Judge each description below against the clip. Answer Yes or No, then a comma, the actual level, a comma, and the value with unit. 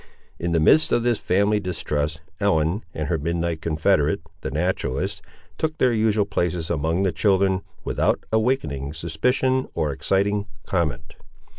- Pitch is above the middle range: No, very low, 90 Hz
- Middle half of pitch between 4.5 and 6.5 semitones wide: Yes, average, 4.8 semitones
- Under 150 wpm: Yes, average, 140 wpm